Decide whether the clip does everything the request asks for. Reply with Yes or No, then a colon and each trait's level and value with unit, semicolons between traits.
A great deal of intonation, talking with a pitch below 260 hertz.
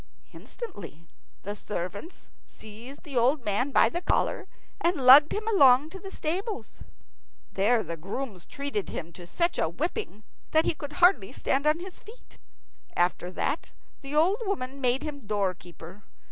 No: wide, 8.5 semitones; very high, 270 Hz